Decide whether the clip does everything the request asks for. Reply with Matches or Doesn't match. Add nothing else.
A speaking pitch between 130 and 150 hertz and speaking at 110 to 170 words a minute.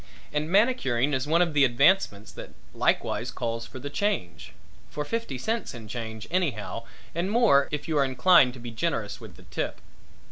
Doesn't match